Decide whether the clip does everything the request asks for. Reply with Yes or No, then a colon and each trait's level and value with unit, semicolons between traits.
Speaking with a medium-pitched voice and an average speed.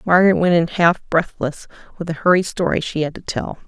No: medium, 170 Hz; fast, 210 wpm